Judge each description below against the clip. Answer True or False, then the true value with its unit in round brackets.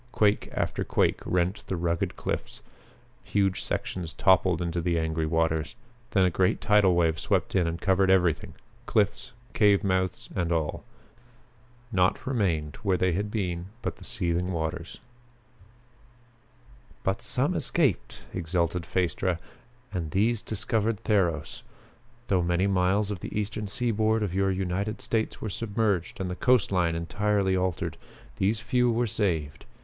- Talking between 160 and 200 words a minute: False (140 wpm)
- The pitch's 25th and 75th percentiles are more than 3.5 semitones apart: False (3.2 semitones)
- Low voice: True (95 Hz)